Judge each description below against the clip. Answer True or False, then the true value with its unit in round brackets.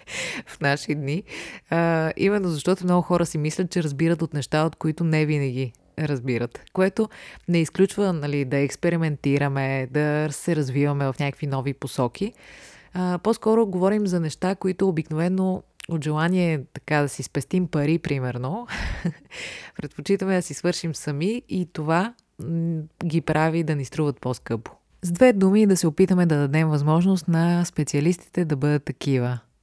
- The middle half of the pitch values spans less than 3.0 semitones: False (3.8 semitones)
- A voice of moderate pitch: True (160 Hz)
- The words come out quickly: False (150 wpm)